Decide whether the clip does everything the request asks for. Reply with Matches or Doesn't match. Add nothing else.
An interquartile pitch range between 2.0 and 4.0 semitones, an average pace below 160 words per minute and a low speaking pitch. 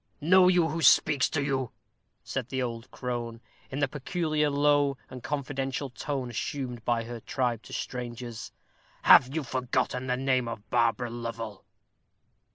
Matches